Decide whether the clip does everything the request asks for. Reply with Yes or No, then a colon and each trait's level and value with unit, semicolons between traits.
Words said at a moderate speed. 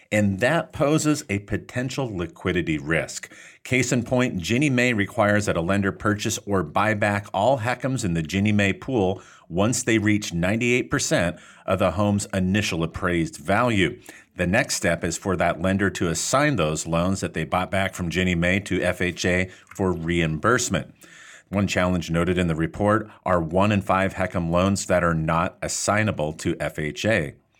Yes: average, 165 wpm